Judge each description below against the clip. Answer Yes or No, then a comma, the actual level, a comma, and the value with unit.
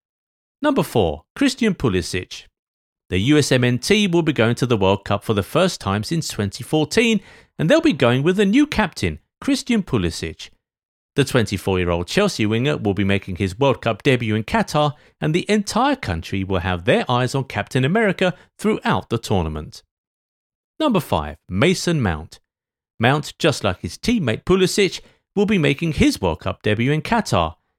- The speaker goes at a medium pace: Yes, average, 160 wpm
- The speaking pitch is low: Yes, low, 130 Hz